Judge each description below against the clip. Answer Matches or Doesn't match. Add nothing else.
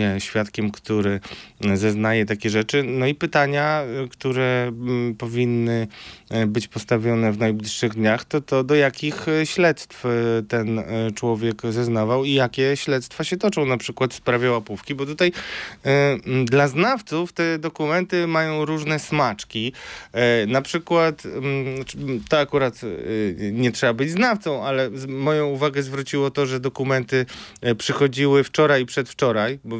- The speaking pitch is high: Doesn't match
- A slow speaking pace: Doesn't match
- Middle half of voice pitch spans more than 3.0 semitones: Matches